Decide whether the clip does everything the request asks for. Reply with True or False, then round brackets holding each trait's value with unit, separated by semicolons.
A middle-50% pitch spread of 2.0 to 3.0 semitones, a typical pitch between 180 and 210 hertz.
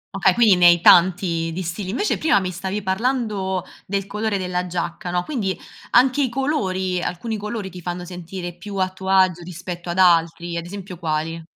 True (2.5 semitones; 185 Hz)